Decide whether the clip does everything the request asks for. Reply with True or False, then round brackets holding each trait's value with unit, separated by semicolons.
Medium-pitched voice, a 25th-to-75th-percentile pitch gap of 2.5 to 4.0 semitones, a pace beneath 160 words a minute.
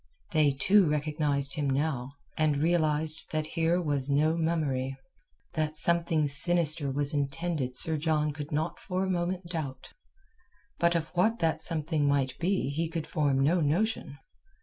True (155 Hz; 2.8 semitones; 150 wpm)